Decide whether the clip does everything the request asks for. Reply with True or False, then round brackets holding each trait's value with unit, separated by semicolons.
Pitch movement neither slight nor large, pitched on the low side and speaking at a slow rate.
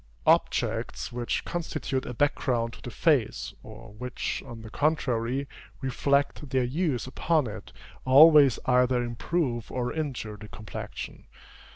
True (3.4 semitones; 125 Hz; 130 wpm)